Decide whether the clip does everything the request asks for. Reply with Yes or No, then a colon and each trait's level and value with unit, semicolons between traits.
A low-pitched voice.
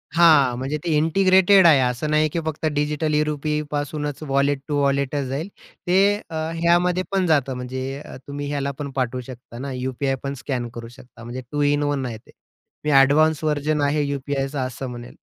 No: medium, 145 Hz